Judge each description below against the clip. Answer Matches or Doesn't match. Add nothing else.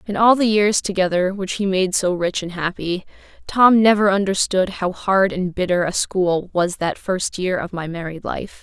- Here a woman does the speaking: Matches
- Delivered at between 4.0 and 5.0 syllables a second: Matches